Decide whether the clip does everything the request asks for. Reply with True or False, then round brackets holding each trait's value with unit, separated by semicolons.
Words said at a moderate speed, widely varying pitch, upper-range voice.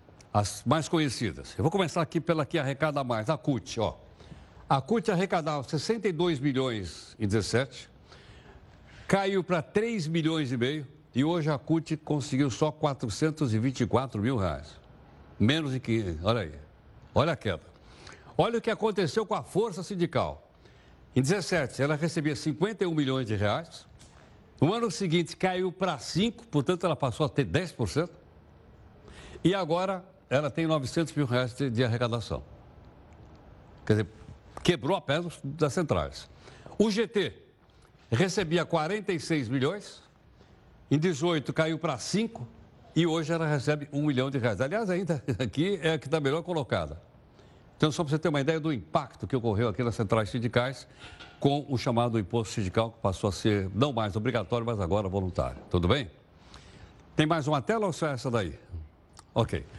False (160 wpm; 6.5 semitones; 145 Hz)